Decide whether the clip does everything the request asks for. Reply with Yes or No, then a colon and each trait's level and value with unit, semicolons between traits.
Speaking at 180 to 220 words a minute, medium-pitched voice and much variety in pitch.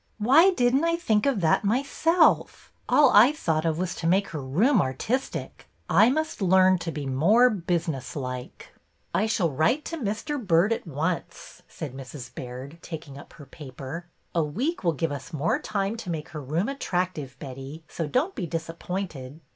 Yes: average, 185 wpm; medium, 170 Hz; wide, 7.2 semitones